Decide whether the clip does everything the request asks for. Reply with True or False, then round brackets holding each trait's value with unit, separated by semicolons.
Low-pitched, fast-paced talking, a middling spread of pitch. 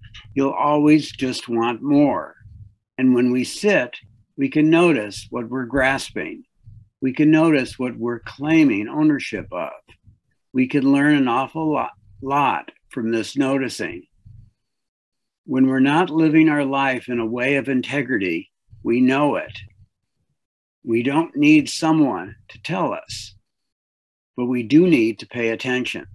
False (130 Hz; 140 wpm; 4.6 semitones)